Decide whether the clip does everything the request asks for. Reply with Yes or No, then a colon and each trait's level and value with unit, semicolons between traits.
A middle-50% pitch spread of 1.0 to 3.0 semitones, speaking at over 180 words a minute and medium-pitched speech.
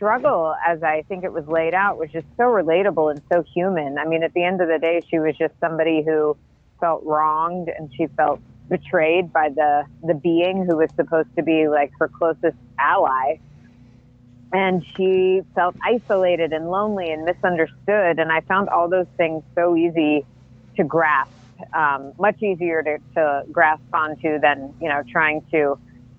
No: narrow, 2.6 semitones; average, 175 wpm; medium, 160 Hz